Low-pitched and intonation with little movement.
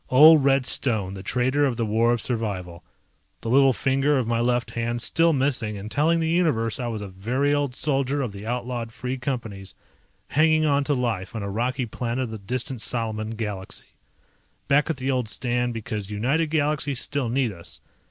No: low, 125 Hz; average, 3.9 semitones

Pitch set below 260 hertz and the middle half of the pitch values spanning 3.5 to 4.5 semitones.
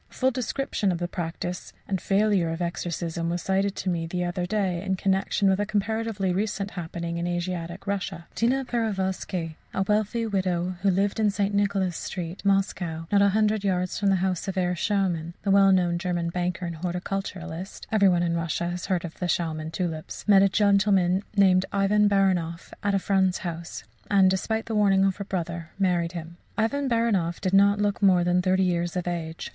No: high, 190 Hz; narrow, 2.5 semitones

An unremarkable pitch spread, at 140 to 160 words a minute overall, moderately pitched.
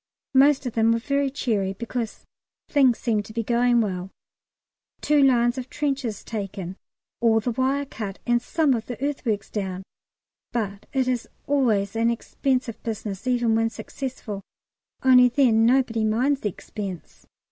No: average, 3.4 semitones; average, 150 wpm; high, 235 Hz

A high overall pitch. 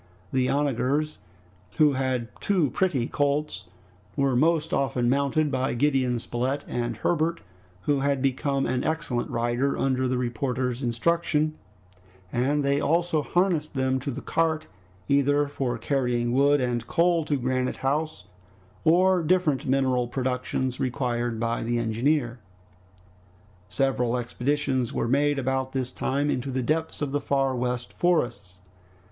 No: low, 135 Hz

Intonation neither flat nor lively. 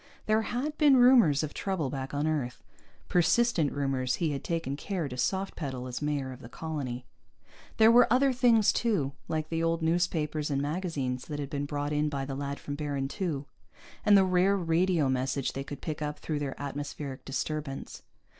Yes: average, 4.6 semitones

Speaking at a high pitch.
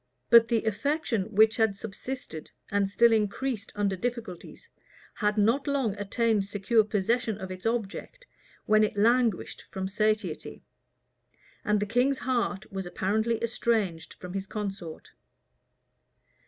Yes: high, 215 Hz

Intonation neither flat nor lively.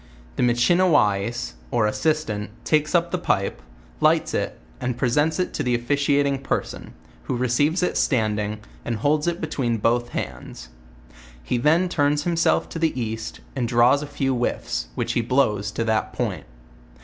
Yes: average, 4.7 semitones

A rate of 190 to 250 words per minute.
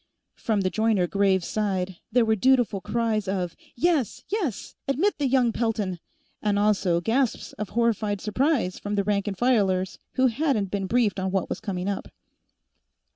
No: average, 165 wpm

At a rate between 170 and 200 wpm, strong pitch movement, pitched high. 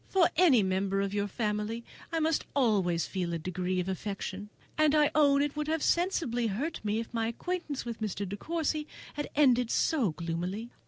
Yes: average, 190 wpm; wide, 7.3 semitones; high, 230 Hz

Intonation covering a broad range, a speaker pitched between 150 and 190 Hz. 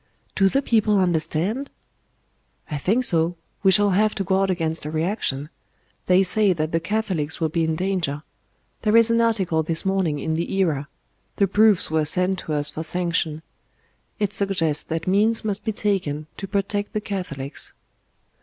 No: average, 4.3 semitones; medium, 185 Hz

